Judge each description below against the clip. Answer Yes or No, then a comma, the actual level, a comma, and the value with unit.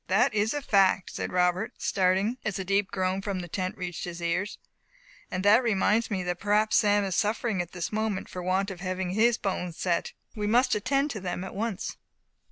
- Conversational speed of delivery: No, fast, 210 wpm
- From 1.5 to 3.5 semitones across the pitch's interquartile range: Yes, average, 2.7 semitones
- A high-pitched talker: Yes, high, 195 Hz